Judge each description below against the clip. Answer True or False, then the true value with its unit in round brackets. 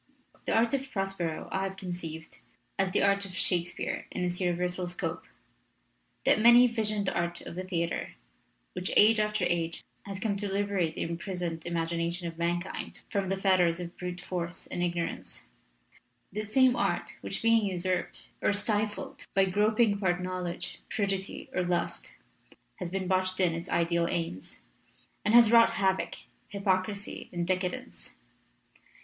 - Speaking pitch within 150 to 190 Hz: True (185 Hz)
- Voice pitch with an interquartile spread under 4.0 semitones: True (2.7 semitones)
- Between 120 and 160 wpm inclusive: True (155 wpm)